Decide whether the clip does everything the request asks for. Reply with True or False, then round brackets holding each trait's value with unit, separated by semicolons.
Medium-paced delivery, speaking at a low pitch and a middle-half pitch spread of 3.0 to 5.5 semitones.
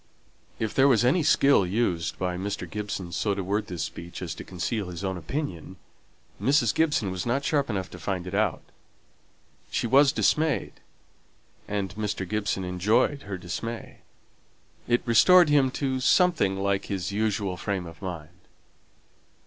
True (155 wpm; 100 Hz; 5.2 semitones)